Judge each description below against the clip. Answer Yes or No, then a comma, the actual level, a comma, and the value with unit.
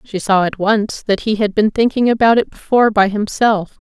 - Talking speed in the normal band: No, fast, 215 wpm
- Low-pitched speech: No, high, 210 Hz